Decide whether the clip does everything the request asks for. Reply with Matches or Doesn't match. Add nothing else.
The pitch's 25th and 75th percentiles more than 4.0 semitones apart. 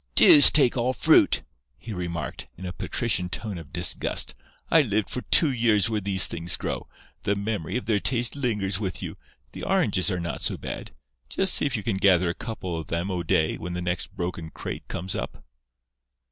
Matches